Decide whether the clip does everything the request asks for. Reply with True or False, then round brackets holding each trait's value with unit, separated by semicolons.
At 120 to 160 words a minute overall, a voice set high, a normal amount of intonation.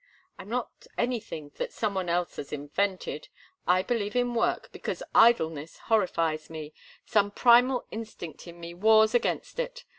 False (150 wpm; 205 Hz; 5.9 semitones)